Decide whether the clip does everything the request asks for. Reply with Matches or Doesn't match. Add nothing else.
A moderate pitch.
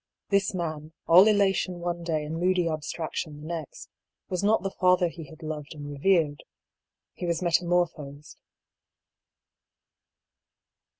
Matches